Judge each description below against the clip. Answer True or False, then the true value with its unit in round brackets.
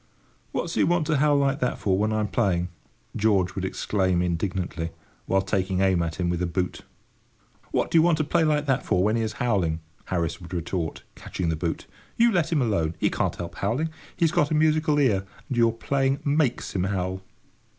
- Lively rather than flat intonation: True (7.9 semitones)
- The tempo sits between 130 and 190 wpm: False (205 wpm)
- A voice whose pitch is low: True (100 Hz)